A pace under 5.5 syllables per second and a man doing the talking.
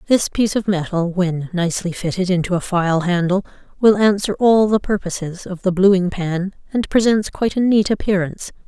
No: 5.2 syllables/s; female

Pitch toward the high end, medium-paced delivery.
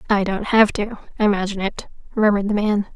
Yes: high, 205 Hz; average, 160 wpm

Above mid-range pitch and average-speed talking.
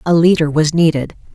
No: medium, 160 Hz; average, 180 wpm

